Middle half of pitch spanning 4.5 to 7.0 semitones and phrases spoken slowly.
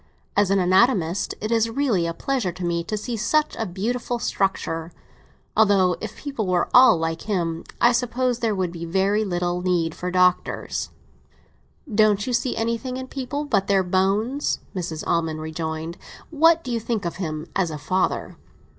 No: average, 5.2 semitones; average, 170 wpm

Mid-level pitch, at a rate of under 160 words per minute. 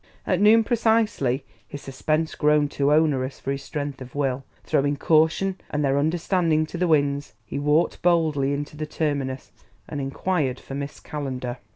No: medium, 145 Hz; average, 165 wpm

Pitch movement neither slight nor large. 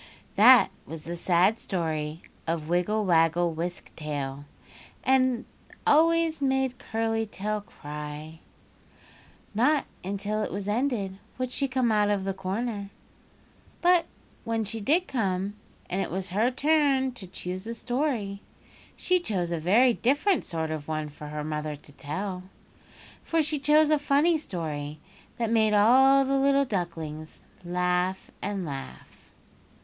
No: wide, 7.2 semitones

